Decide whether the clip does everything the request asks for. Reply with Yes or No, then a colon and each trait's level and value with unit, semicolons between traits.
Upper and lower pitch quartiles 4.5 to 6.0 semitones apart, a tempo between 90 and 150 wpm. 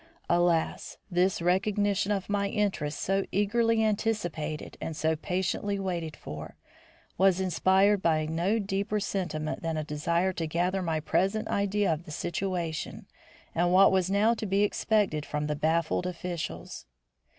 No: average, 3.7 semitones; average, 145 wpm